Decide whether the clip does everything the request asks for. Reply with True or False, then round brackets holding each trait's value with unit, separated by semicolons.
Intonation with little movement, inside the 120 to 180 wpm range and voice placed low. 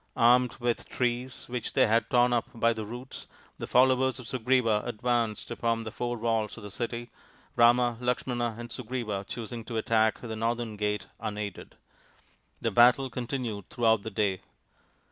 True (1.8 semitones; 160 wpm; 120 Hz)